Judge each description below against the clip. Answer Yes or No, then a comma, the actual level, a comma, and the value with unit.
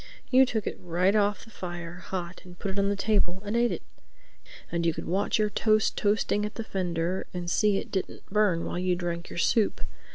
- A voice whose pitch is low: No, high, 190 Hz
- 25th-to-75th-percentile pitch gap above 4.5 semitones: No, average, 3.2 semitones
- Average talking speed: No, fast, 220 wpm